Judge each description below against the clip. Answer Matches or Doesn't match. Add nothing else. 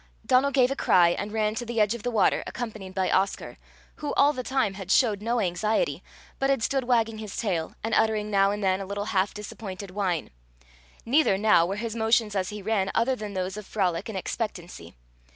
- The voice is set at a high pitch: Matches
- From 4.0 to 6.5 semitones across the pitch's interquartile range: Doesn't match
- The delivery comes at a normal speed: Doesn't match